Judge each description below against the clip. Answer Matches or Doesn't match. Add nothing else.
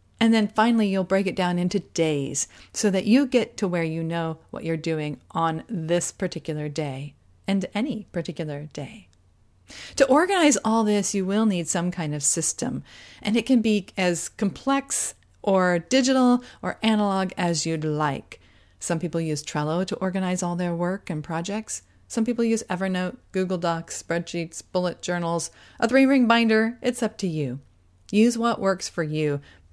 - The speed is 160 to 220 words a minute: Matches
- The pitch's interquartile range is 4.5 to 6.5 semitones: Matches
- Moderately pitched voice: Matches